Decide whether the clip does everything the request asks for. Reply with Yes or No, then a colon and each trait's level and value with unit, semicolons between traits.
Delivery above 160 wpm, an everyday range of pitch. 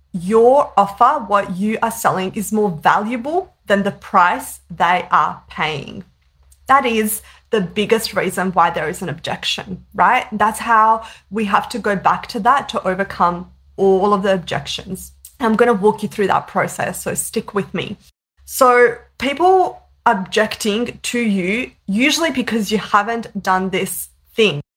No: average, 155 wpm; average, 3.9 semitones